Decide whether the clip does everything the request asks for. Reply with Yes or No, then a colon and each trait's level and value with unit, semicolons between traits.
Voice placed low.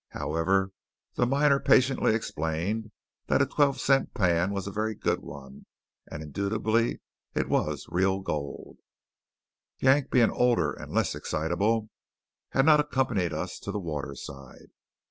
Yes: low, 100 Hz